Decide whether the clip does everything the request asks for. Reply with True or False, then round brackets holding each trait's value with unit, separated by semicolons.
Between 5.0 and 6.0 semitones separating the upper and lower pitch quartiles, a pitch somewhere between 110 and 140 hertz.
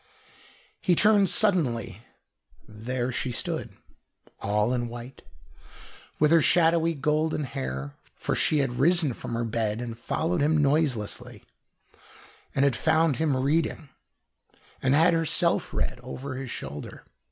True (5.3 semitones; 135 Hz)